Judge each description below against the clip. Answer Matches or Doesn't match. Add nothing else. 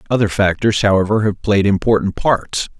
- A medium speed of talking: Matches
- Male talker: Matches